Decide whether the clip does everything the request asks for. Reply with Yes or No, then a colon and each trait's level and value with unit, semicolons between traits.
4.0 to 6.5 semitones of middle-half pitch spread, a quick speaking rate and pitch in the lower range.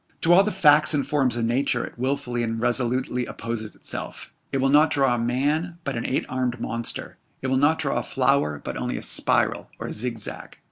No: average, 3.3 semitones; fast, 215 wpm; low, 130 Hz